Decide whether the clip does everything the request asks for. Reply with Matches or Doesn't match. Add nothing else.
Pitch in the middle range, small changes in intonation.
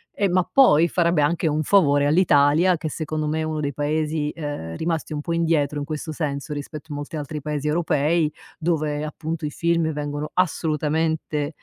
Matches